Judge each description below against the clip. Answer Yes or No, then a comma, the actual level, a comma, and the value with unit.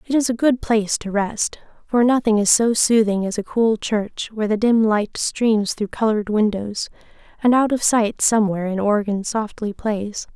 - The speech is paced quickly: No, average, 190 wpm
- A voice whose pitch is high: Yes, high, 215 Hz